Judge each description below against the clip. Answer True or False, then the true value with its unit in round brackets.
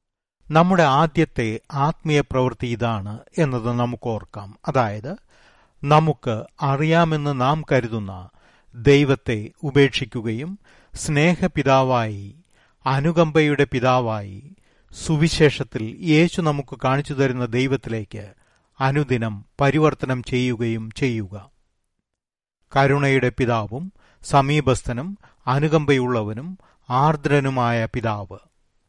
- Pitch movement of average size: True (4.5 semitones)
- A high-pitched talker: False (130 Hz)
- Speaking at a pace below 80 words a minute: True (70 wpm)